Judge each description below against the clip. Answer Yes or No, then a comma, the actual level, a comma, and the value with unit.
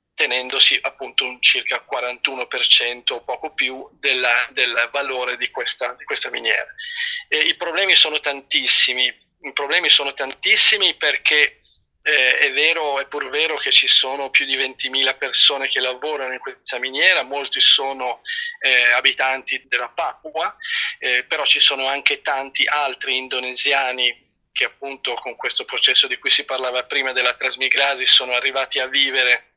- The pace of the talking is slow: No, average, 145 wpm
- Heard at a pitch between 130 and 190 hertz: Yes, medium, 140 Hz